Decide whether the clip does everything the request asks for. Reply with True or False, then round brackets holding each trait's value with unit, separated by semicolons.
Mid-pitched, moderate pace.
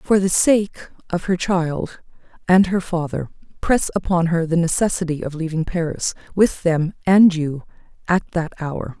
True (170 Hz; 160 wpm)